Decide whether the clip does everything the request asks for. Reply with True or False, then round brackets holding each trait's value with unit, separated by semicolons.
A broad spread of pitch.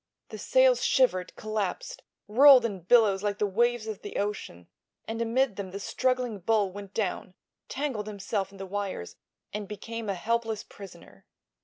False (3.0 semitones)